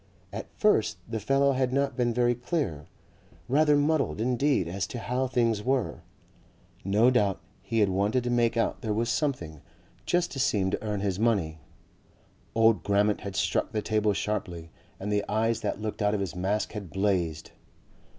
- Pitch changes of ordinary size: Yes, average, 3.9 semitones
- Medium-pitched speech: No, low, 110 Hz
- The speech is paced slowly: No, average, 175 wpm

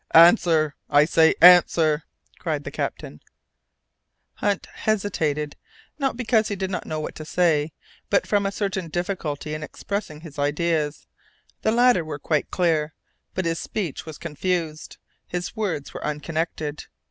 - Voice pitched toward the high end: No, medium, 165 Hz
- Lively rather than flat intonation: No, average, 4.0 semitones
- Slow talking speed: No, average, 145 wpm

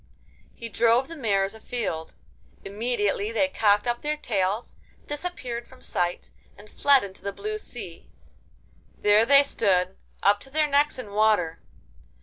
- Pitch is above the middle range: Yes, high, 225 Hz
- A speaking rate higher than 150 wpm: No, average, 140 wpm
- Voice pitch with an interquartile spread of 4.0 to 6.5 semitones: Yes, wide, 5.5 semitones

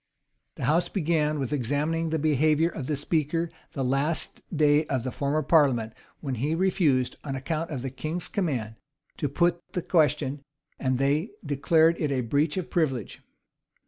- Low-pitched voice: No, medium, 150 Hz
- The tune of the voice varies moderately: Yes, average, 3.2 semitones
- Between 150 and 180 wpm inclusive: Yes, average, 170 wpm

